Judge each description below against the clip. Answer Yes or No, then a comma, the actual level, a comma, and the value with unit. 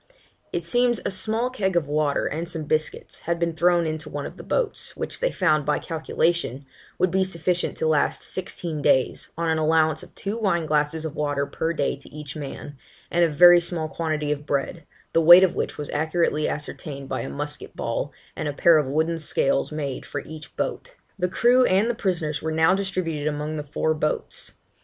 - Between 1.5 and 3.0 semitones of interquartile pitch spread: Yes, average, 2.7 semitones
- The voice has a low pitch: No, medium, 160 Hz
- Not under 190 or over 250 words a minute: Yes, fast, 205 wpm